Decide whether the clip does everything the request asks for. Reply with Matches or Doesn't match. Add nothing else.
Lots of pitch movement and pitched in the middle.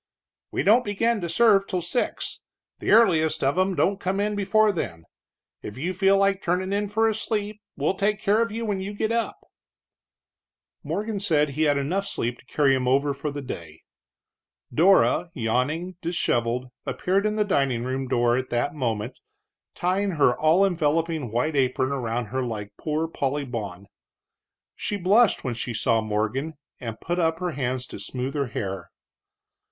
Matches